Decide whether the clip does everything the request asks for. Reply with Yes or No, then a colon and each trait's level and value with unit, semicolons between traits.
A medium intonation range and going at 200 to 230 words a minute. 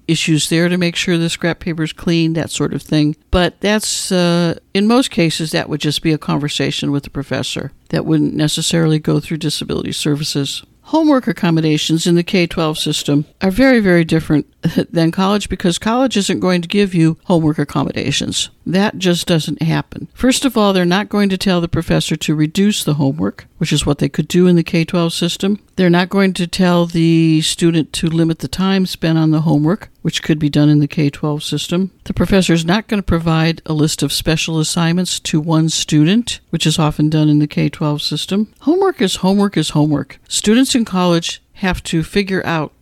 Yes: average, 3.1 semitones; fast, 205 wpm